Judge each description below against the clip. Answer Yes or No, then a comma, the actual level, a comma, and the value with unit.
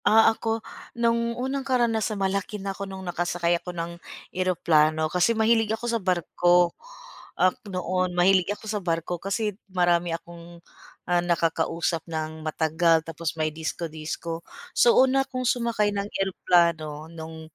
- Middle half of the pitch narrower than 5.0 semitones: Yes, average, 4.2 semitones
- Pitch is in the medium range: Yes, medium, 180 Hz